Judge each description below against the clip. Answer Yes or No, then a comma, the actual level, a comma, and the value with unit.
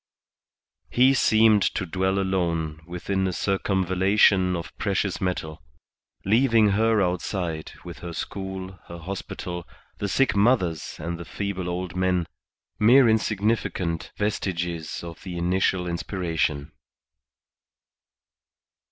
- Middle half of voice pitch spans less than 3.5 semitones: Yes, average, 2.8 semitones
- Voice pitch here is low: Yes, very low, 95 Hz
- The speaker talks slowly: Yes, slow, 110 wpm